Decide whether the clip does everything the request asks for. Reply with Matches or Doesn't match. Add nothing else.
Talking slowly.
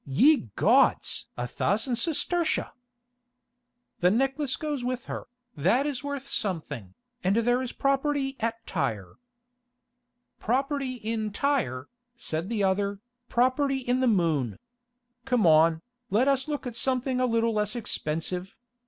Matches